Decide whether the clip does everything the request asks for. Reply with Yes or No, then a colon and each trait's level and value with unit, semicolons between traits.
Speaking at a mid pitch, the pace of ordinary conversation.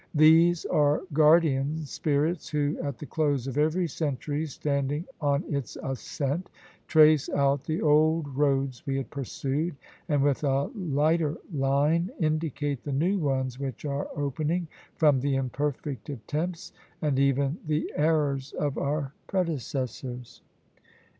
No: medium, 145 Hz; slow, 130 wpm